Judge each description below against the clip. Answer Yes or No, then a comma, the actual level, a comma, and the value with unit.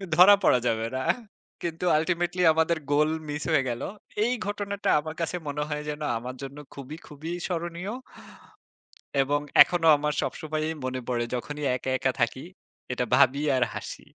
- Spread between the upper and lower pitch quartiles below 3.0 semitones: No, average, 4.3 semitones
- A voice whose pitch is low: No, medium, 150 Hz